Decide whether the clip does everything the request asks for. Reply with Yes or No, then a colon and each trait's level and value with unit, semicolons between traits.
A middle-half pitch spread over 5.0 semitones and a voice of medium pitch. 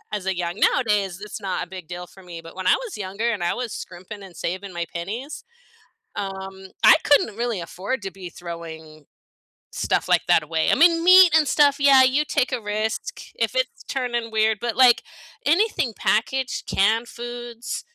No: wide, 5.6 semitones; high, 215 Hz